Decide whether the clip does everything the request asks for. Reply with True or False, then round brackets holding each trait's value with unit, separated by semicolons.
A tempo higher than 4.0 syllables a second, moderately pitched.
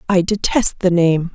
True (4.3 syllables/s; 180 Hz)